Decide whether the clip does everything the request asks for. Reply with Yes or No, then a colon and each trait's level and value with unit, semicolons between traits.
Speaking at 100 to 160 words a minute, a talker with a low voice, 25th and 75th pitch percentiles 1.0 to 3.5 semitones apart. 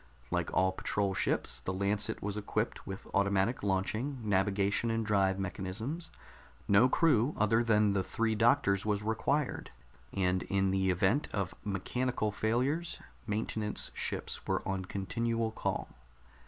Yes: slow, 135 wpm; low, 105 Hz; average, 3.0 semitones